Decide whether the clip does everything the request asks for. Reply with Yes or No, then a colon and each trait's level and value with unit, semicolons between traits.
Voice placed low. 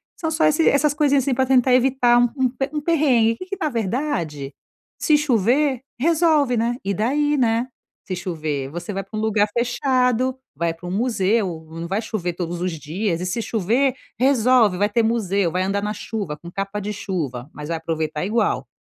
No: high, 220 Hz